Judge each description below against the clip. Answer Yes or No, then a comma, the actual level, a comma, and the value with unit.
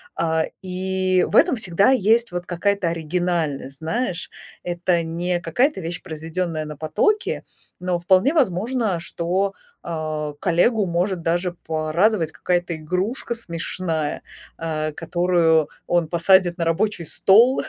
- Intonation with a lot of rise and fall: No, average, 2.7 semitones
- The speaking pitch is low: No, medium, 175 Hz